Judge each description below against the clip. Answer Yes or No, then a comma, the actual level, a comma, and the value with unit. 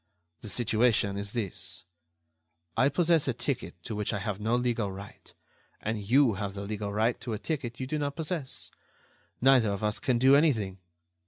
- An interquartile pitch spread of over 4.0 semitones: Yes, average, 4.6 semitones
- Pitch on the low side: Yes, low, 115 Hz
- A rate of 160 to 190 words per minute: Yes, average, 180 wpm